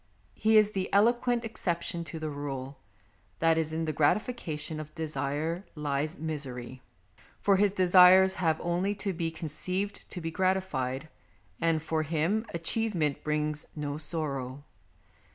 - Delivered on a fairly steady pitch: No, average, 3.9 semitones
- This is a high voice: No, medium, 160 Hz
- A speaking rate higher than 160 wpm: No, slow, 135 wpm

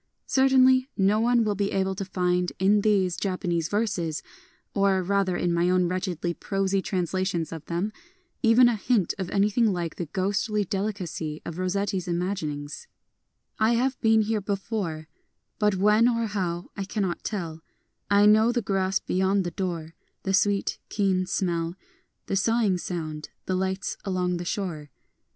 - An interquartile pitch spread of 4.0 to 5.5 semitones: No, average, 2.9 semitones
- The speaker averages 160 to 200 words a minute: Yes, average, 165 wpm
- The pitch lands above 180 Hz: Yes, high, 190 Hz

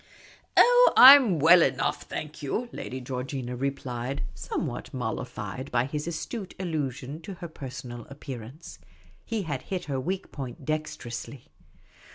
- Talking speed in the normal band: Yes, average, 150 wpm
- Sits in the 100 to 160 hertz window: Yes, medium, 140 Hz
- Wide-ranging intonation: No, average, 4.9 semitones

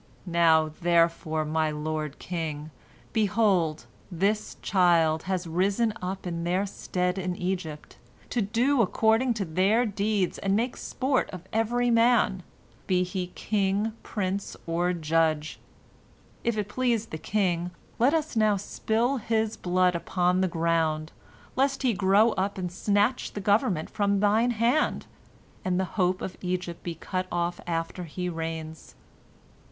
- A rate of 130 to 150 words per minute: Yes, average, 140 wpm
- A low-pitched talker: No, medium, 185 Hz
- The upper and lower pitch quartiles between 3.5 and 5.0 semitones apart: Yes, average, 4.3 semitones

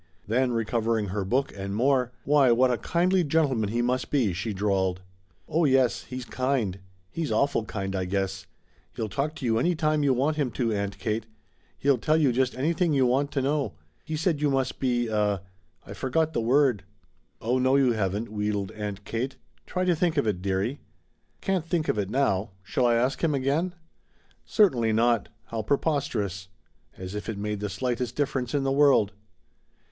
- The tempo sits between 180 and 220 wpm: Yes, average, 185 wpm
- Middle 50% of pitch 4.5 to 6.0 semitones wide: Yes, average, 5.2 semitones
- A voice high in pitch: No, low, 125 Hz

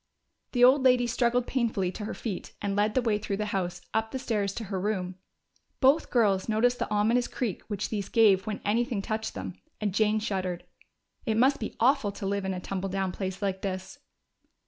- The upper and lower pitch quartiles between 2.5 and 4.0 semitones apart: Yes, average, 3.6 semitones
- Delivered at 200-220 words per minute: Yes, fast, 205 wpm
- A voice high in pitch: Yes, high, 210 Hz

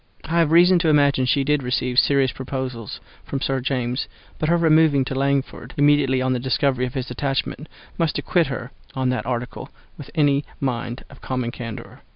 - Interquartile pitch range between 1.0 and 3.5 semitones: Yes, narrow, 2.4 semitones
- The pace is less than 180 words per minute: No, average, 185 wpm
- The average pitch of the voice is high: No, low, 135 Hz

